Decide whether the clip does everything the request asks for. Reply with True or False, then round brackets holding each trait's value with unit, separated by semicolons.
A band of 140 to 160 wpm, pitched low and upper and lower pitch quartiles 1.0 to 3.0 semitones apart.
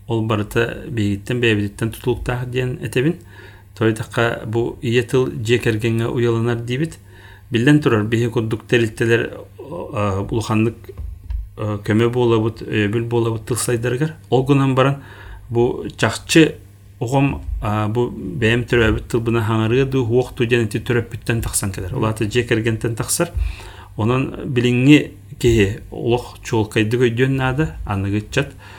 False (110 wpm; 115 Hz; 2.7 semitones)